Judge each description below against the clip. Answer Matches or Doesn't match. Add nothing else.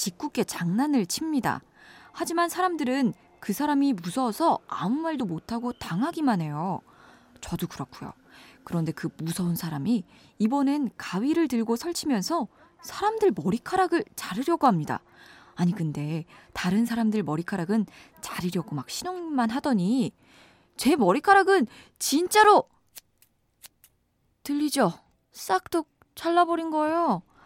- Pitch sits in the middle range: Doesn't match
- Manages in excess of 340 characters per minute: Doesn't match